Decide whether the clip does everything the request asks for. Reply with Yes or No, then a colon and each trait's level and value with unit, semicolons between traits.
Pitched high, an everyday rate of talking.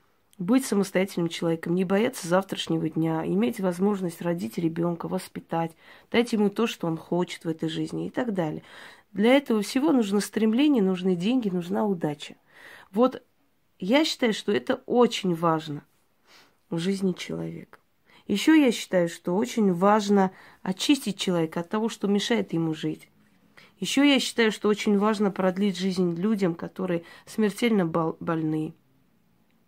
Yes: high, 195 Hz; average, 140 wpm